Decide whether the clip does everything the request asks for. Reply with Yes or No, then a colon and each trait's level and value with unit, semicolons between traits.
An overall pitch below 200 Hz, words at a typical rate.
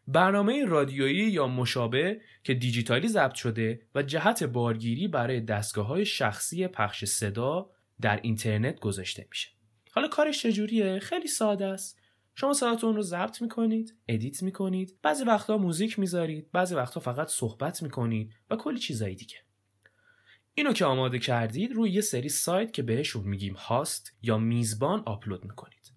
Yes: medium, 140 Hz; average, 145 wpm